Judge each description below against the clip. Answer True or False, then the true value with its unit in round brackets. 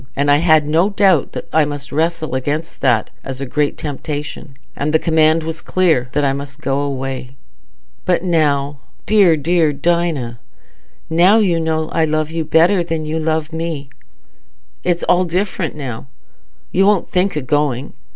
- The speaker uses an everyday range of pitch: True (3.0 semitones)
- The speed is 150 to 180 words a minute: True (165 wpm)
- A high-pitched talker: False (155 Hz)